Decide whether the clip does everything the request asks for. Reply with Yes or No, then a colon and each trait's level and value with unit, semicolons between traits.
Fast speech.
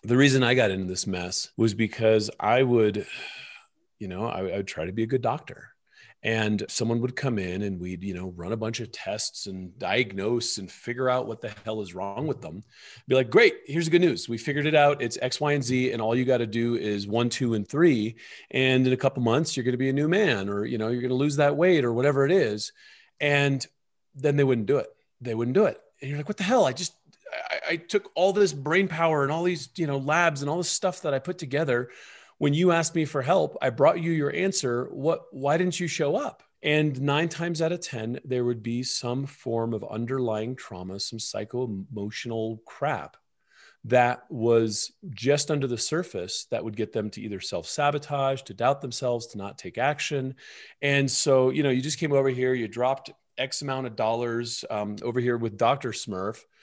Yes: fast, 230 wpm